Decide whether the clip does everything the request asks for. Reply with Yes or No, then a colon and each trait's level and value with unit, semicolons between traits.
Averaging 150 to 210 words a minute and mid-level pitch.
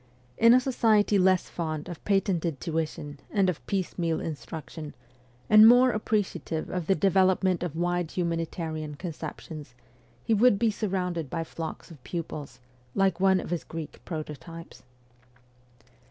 No: average, 140 wpm; medium, 175 Hz